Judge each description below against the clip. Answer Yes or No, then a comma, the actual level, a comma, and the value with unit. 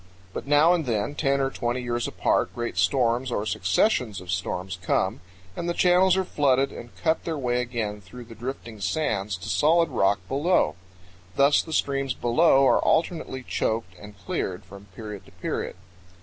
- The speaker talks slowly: No, average, 175 wpm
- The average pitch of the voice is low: Yes, low, 120 Hz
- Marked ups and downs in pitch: Yes, wide, 6.1 semitones